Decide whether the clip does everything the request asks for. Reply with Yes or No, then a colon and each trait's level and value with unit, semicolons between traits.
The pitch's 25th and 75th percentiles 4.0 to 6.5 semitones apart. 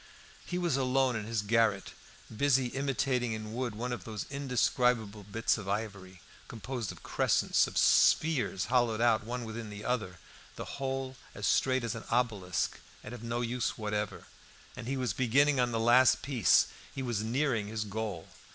No: average, 3.1 semitones